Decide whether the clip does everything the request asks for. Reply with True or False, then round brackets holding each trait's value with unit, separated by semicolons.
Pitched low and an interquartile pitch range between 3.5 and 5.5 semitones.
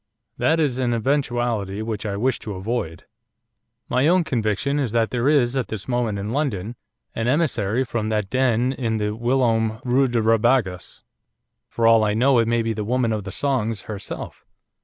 False (115 Hz; 3.1 semitones)